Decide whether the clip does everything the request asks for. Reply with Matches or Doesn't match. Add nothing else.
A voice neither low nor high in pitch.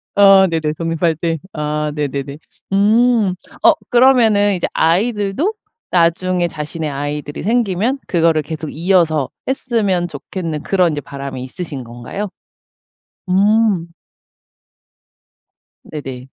Matches